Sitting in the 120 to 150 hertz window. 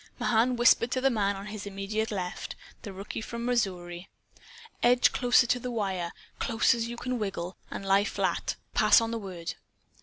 No: high, 215 Hz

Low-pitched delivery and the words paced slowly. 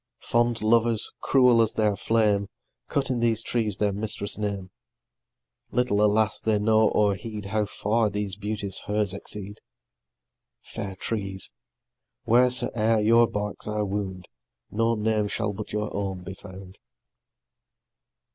Yes: low, 105 Hz; slow, 130 wpm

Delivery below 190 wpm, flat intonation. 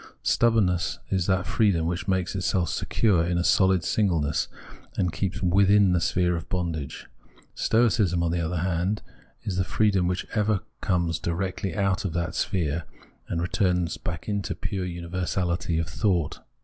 Yes: average, 160 wpm; narrow, 2.2 semitones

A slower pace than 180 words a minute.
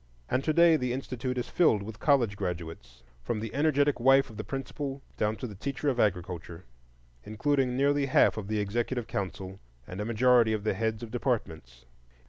No: average, 185 wpm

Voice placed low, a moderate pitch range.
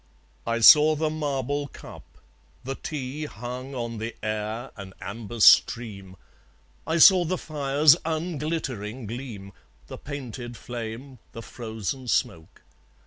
Yes: low, 125 Hz; average, 4.7 semitones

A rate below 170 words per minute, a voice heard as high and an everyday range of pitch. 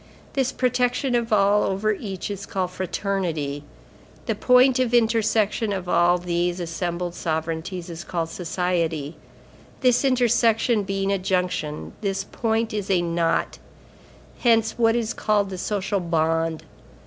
Yes: slow, 135 wpm; high, 195 Hz; average, 4.6 semitones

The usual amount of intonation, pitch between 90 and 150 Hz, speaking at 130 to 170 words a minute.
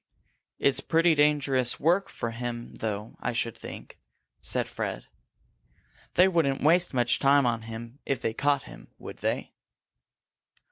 Yes: average, 4.1 semitones; low, 135 Hz; average, 140 wpm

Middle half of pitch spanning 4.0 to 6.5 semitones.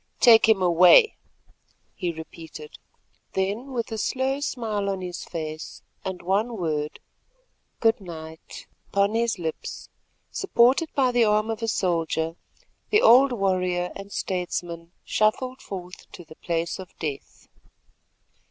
Yes: average, 5.1 semitones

